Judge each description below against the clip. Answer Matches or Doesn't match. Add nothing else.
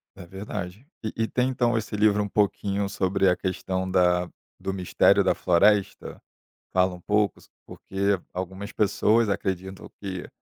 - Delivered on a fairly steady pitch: Matches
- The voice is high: Doesn't match